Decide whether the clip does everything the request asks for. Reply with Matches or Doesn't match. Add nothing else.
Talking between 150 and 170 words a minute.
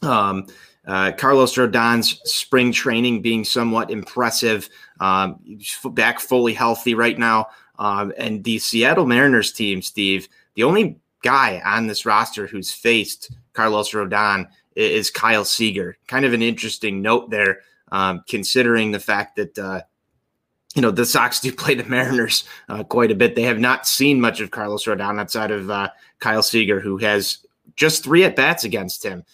Matches